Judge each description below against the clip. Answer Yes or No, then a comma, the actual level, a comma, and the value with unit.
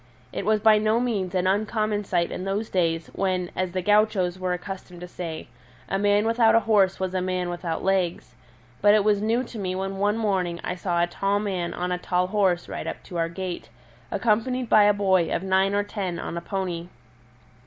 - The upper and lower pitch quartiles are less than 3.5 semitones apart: Yes, average, 2.7 semitones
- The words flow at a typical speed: No, fast, 215 wpm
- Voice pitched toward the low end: No, high, 190 Hz